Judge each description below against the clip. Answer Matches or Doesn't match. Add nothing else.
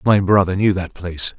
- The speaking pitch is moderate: Doesn't match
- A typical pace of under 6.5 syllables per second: Matches